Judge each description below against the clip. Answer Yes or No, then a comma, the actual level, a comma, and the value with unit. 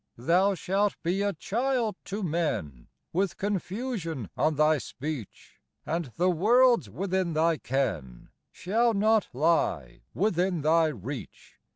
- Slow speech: Yes, slow, 120 wpm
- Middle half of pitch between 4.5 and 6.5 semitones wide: Yes, average, 4.9 semitones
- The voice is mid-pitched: Yes, medium, 175 Hz